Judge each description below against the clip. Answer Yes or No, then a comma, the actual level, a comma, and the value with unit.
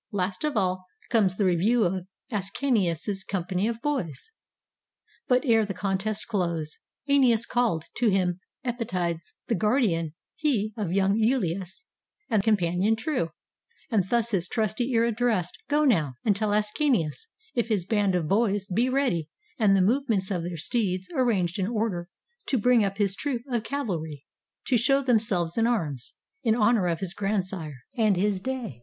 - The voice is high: Yes, high, 205 Hz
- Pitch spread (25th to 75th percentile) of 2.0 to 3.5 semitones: No, average, 4.5 semitones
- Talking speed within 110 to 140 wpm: No, average, 165 wpm